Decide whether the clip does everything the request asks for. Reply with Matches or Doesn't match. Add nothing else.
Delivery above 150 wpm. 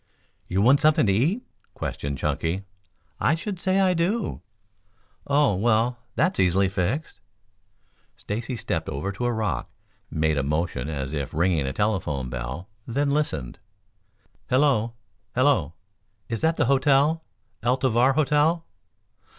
Doesn't match